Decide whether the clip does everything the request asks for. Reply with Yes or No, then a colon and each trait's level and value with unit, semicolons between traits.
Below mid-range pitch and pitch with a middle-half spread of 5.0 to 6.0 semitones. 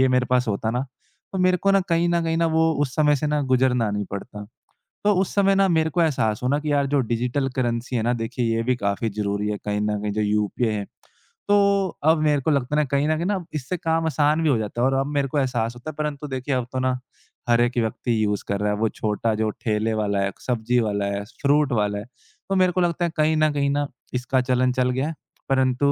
Yes: low, 130 Hz; wide, 5.5 semitones